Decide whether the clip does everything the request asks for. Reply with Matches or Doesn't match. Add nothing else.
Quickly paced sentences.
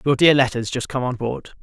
Matches